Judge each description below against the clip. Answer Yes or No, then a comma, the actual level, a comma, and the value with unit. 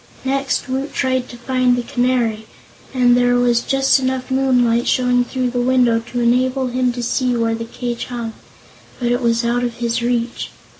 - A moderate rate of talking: Yes, average, 185 wpm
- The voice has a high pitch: Yes, high, 245 Hz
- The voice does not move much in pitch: Yes, narrow, 1.4 semitones